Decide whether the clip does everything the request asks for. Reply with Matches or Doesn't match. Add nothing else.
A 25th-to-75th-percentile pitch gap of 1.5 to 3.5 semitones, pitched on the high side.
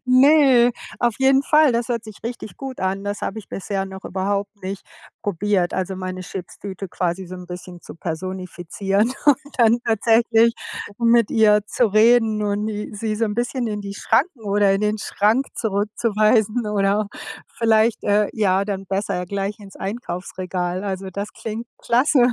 Matches